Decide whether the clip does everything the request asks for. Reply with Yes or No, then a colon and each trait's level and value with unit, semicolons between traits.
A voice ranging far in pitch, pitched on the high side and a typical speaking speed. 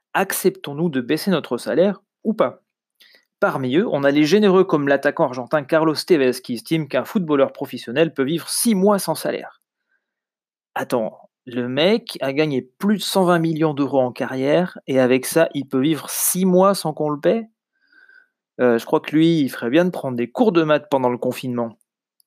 No: wide, 6.0 semitones; medium, 155 Hz; average, 190 wpm